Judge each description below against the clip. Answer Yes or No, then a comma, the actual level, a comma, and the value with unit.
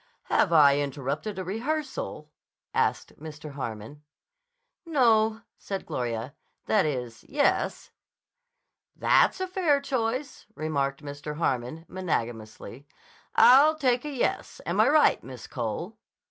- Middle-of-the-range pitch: Yes, medium, 165 Hz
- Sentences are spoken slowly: Yes, slow, 110 wpm